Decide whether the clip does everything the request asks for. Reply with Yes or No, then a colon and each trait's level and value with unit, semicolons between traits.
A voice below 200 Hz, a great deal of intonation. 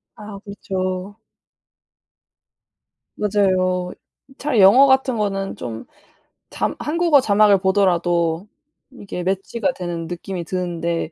No: high, 190 Hz; average, 2.9 semitones